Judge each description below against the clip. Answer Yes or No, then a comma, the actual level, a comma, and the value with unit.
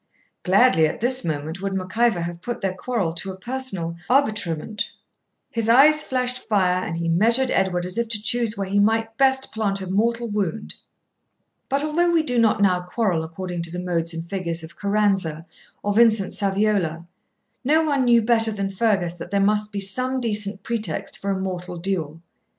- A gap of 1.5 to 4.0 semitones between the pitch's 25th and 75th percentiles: No, average, 4.6 semitones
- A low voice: No, high, 200 Hz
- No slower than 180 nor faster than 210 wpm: Yes, average, 185 wpm